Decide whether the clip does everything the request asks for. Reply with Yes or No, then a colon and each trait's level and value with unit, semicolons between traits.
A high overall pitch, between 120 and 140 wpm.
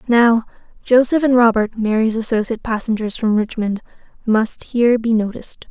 Yes: high, 225 Hz; slow, 135 wpm